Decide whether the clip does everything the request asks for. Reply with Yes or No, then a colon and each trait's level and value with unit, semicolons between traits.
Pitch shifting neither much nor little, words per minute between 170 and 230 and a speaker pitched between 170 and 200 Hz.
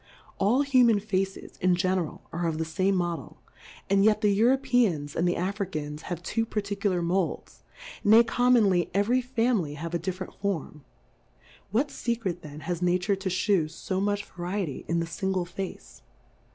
Yes: average, 3.5 semitones; average, 175 wpm; high, 190 Hz